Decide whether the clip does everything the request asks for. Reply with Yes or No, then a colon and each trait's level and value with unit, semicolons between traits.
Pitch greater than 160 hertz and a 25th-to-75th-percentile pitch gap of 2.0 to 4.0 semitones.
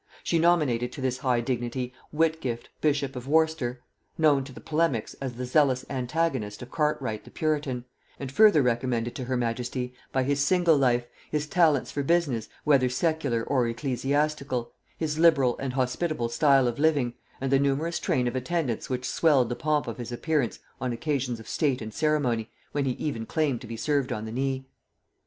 No: low, 135 Hz; average, 3.7 semitones